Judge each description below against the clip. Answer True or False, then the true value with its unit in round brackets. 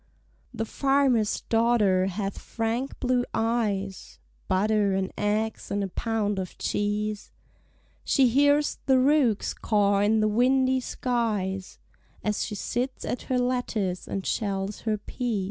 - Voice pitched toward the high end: True (220 Hz)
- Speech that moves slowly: True (130 wpm)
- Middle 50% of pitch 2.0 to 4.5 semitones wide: True (3.5 semitones)